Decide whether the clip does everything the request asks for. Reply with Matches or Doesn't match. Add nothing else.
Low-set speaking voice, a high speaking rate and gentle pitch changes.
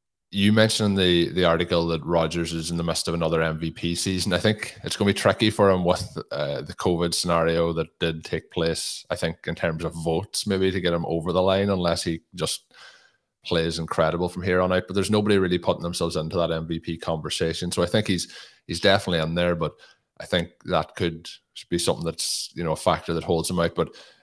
Matches